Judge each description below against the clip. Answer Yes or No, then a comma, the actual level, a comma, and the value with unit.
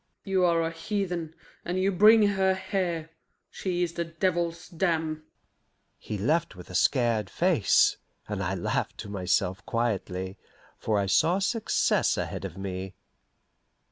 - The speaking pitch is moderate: Yes, medium, 165 Hz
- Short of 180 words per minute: Yes, average, 140 wpm